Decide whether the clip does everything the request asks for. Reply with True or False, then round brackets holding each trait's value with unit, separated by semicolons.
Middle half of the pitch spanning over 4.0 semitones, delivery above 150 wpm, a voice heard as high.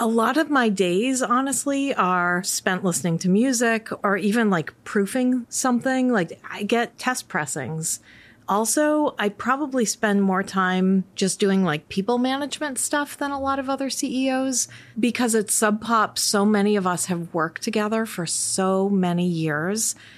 True (5.3 semitones; 160 wpm; 215 Hz)